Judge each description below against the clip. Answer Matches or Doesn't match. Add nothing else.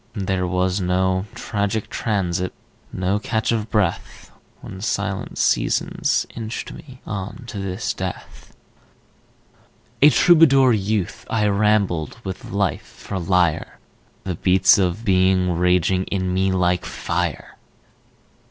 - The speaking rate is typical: Doesn't match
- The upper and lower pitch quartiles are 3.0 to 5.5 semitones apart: Doesn't match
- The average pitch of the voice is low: Matches